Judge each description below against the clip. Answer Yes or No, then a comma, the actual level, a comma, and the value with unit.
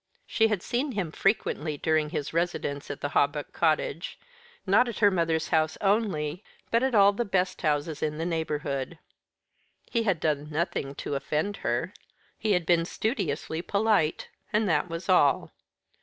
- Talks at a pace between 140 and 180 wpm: Yes, average, 160 wpm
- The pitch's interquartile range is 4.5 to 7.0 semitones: Yes, average, 5.0 semitones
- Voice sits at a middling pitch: Yes, medium, 165 Hz